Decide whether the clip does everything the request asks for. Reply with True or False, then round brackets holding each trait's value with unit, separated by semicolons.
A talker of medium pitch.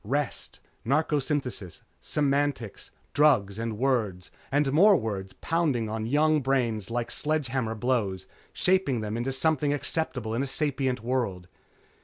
False (130 Hz)